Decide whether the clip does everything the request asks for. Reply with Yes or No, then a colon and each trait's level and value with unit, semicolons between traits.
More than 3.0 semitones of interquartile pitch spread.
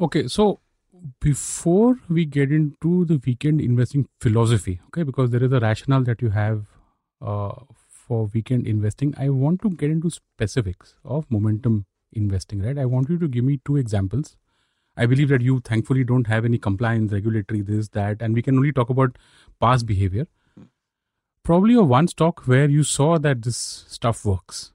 Yes: average, 4.9 semitones